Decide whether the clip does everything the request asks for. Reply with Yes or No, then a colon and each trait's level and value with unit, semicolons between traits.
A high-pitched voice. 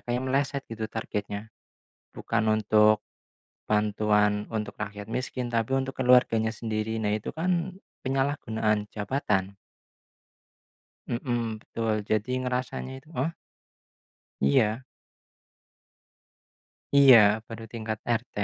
No: low, 115 Hz